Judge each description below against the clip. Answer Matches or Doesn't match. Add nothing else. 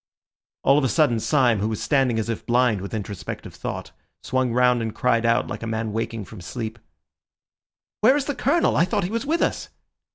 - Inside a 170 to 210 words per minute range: Matches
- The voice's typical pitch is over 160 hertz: Doesn't match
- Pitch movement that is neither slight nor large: Matches